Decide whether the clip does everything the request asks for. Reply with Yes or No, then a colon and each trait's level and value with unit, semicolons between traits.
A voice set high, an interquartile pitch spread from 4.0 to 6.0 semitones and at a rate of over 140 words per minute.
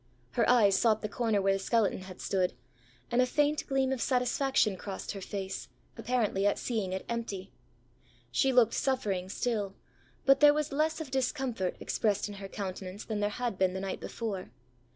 Yes: high, 215 Hz; average, 4.6 semitones; average, 180 wpm